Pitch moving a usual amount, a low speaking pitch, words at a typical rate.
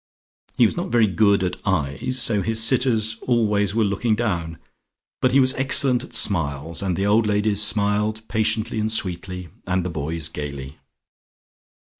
Yes: average, 3.7 semitones; low, 105 Hz; average, 160 wpm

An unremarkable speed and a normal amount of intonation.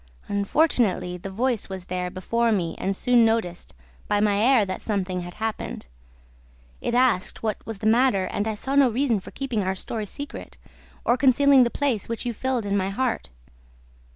Yes: average, 180 wpm; average, 4.4 semitones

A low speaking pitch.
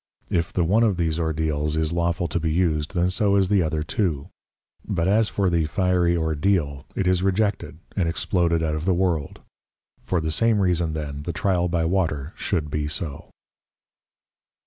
Yes: very low, 85 Hz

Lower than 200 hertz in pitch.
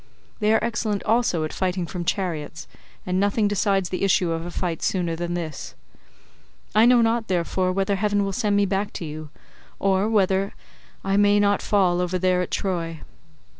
Yes: high, 190 Hz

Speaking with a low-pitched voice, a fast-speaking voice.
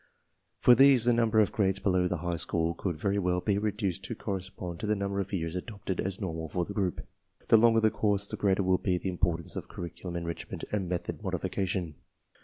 Yes: very low, 95 Hz; fast, 220 wpm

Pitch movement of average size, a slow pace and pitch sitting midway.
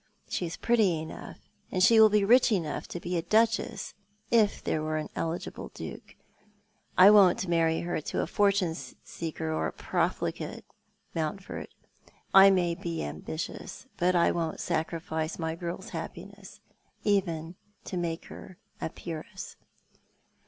No: average, 3.4 semitones; average, 145 wpm; medium, 175 Hz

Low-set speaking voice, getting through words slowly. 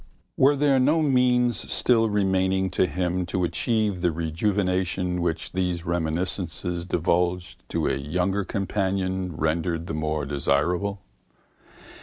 Yes: very low, 90 Hz; slow, 120 wpm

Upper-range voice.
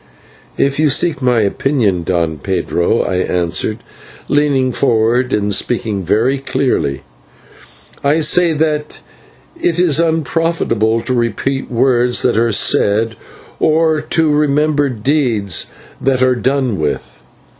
No: low, 125 Hz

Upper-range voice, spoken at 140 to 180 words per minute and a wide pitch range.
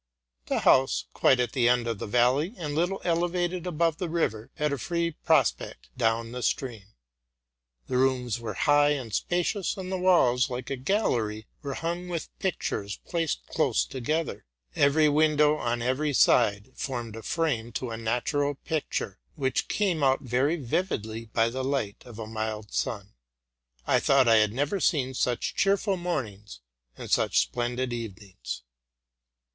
No: low, 130 Hz; average, 160 wpm; wide, 5.7 semitones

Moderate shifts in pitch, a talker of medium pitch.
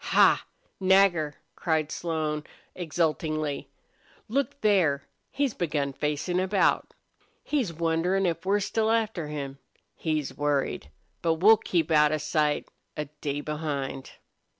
Yes: average, 4.0 semitones; medium, 160 Hz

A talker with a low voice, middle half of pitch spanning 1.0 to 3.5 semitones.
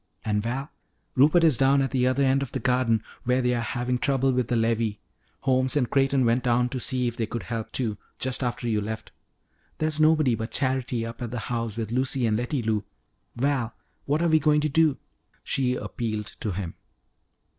Yes: low, 125 Hz; average, 2.8 semitones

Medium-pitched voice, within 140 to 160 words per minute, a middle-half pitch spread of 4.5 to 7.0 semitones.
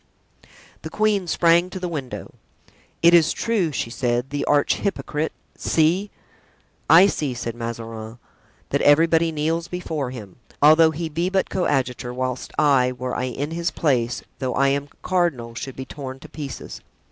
Yes: medium, 145 Hz; average, 155 wpm; average, 4.8 semitones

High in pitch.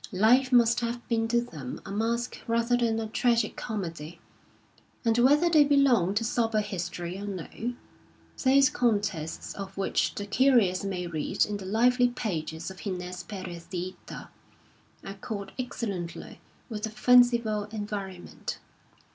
Yes: high, 215 Hz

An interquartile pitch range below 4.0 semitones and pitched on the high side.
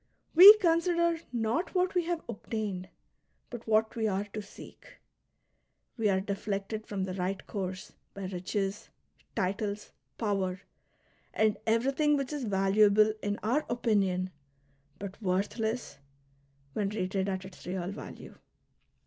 Yes: average, 3.5 semitones; high, 210 Hz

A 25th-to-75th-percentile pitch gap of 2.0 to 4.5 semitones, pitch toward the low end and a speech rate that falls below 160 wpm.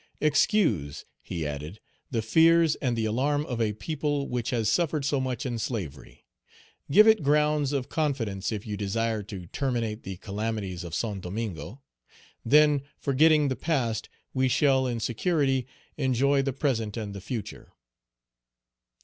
No: average, 5.2 semitones; low, 125 Hz; average, 150 wpm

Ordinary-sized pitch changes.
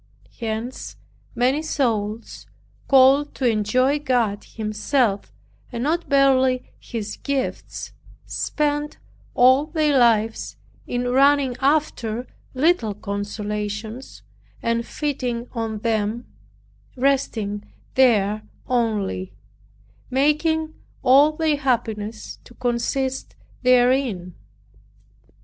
Yes: average, 4.0 semitones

